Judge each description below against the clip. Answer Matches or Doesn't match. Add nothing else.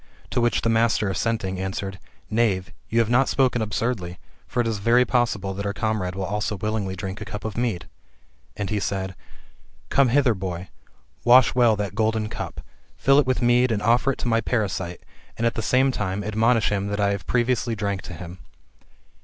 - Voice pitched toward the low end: Matches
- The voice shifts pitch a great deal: Doesn't match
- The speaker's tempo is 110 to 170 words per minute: Doesn't match